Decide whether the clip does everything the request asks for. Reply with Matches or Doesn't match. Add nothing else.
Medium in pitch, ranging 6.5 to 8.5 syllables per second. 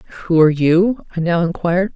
Matches